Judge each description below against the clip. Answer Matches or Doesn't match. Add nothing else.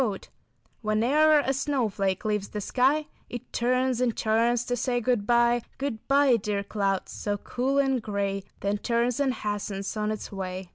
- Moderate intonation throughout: Matches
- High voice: Matches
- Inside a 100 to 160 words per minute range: Doesn't match